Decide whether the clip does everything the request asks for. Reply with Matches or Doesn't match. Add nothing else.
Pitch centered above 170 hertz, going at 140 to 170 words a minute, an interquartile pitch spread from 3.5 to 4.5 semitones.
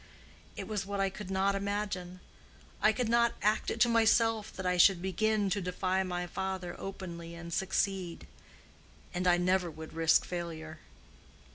Doesn't match